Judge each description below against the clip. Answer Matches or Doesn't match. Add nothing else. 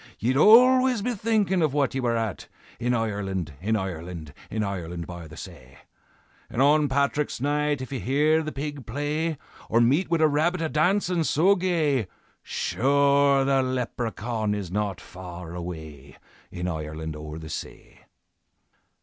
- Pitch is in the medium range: Doesn't match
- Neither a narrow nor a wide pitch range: Doesn't match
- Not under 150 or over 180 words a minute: Matches